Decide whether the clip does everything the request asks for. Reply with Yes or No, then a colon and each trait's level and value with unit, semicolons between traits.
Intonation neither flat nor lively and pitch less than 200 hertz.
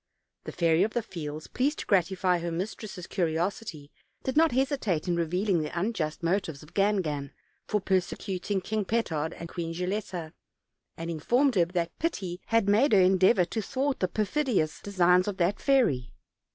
Yes: average, 4.3 semitones; medium, 185 Hz